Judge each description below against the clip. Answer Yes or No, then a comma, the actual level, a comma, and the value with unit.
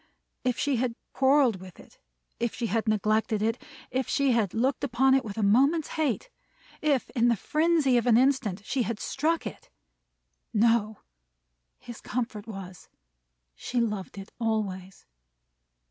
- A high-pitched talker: Yes, high, 235 Hz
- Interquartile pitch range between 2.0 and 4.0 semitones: Yes, average, 3.7 semitones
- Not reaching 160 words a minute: Yes, average, 150 wpm